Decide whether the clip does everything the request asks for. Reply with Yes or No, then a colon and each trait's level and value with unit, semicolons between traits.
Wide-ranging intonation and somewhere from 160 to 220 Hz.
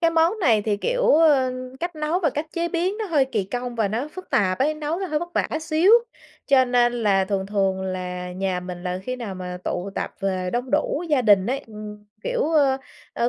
No: wide, 8.0 semitones; high, 245 Hz